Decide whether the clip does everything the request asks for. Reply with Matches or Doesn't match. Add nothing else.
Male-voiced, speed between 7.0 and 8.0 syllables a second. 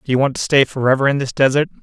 Matches